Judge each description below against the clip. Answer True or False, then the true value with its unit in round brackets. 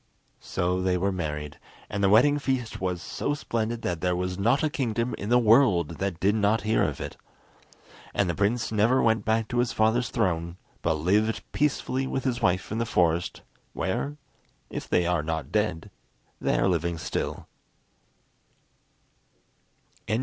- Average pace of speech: True (165 wpm)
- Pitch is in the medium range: False (105 Hz)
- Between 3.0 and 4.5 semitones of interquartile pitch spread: False (4.9 semitones)